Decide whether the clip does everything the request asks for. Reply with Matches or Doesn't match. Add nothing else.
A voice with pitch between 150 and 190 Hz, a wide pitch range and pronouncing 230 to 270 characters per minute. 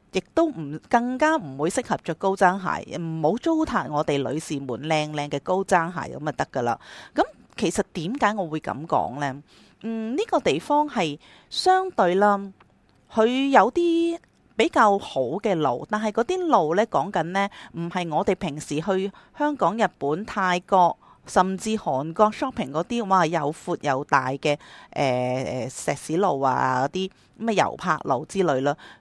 Matches